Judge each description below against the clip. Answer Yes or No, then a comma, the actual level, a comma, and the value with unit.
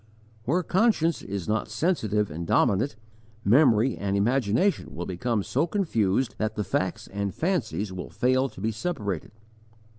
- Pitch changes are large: Yes, wide, 6.2 semitones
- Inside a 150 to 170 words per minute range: No, average, 140 wpm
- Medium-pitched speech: No, low, 110 Hz